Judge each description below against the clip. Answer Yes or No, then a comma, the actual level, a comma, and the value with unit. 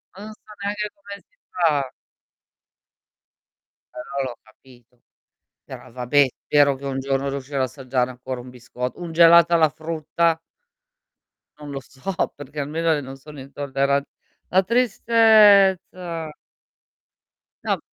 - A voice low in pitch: No, medium, 145 Hz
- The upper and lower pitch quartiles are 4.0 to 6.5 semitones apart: Yes, average, 4.5 semitones